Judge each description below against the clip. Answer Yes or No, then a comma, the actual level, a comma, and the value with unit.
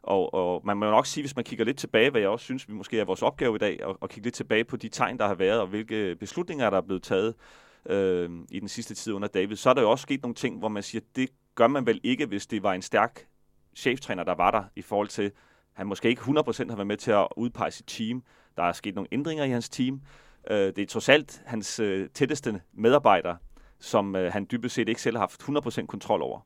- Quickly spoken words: Yes, fast, 270 wpm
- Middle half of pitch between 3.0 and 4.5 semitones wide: Yes, average, 3.7 semitones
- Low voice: Yes, low, 110 Hz